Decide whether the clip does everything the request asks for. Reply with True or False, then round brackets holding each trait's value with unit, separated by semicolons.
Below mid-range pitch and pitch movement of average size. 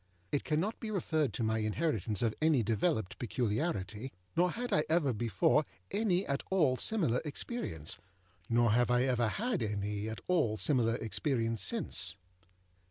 False (125 Hz; 6.9 semitones)